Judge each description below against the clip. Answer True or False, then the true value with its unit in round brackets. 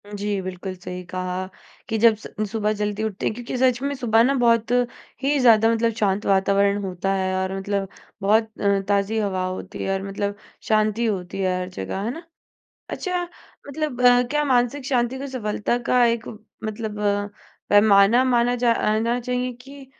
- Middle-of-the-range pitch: False (215 Hz)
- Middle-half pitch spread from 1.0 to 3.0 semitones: False (3.7 semitones)